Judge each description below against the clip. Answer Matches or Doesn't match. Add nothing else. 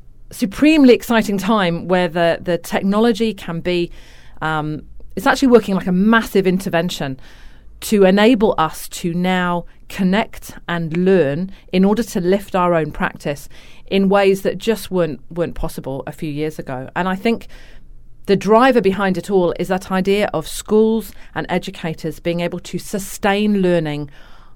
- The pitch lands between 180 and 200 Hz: Matches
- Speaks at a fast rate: Doesn't match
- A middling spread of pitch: Matches